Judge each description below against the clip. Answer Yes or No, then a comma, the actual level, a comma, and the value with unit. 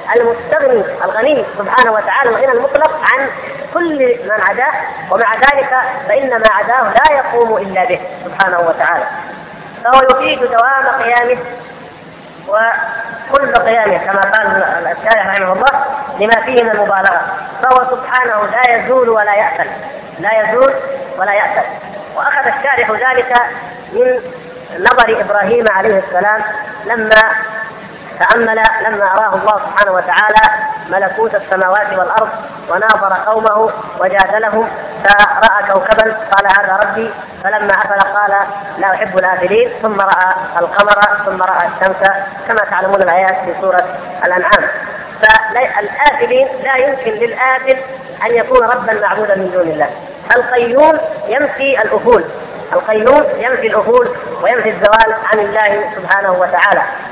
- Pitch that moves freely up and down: No, average, 4.9 semitones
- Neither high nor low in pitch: No, high, 220 Hz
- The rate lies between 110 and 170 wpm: Yes, average, 120 wpm